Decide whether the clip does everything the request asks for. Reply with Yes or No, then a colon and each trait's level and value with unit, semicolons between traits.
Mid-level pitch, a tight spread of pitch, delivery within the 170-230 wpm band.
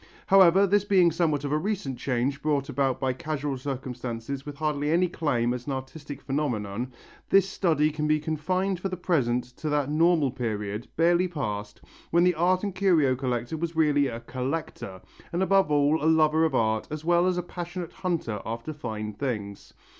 No: medium, 150 Hz; average, 5.1 semitones; average, 185 wpm